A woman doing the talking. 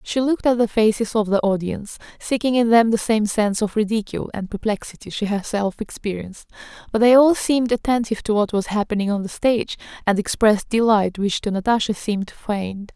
Yes: female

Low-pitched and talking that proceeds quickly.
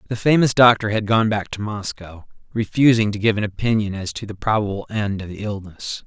Yes: low, 105 Hz; fast, 210 wpm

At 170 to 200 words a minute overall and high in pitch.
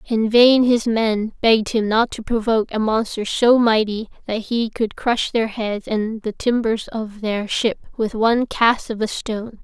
Yes: average, 195 wpm; high, 225 Hz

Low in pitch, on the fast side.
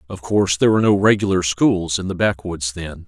Yes: very low, 90 Hz; fast, 215 wpm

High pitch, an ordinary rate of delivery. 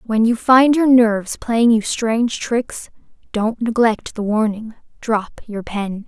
Yes: high, 225 Hz; average, 150 wpm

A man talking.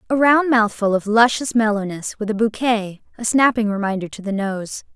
No: female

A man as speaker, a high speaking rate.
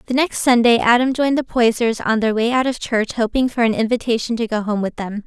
No: female; fast, 250 wpm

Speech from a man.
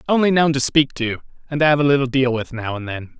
Yes: male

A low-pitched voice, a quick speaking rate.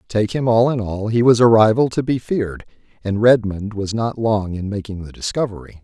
Yes: low, 110 Hz; fast, 215 wpm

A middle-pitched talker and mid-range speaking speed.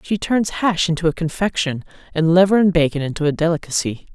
Yes: medium, 170 Hz; average, 190 wpm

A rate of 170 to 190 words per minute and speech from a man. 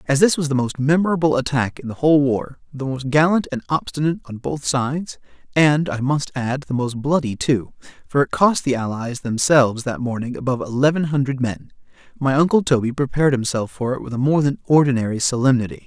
Yes: average, 185 wpm; male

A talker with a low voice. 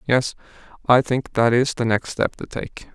Yes: low, 120 Hz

